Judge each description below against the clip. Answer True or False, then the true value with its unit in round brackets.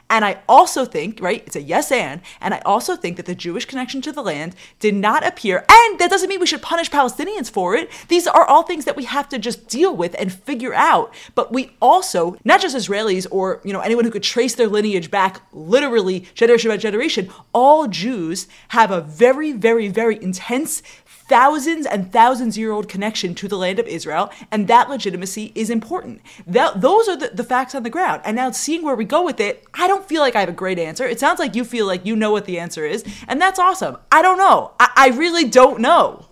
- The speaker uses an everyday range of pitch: False (6.2 semitones)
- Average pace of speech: False (230 wpm)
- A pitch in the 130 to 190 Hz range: False (235 Hz)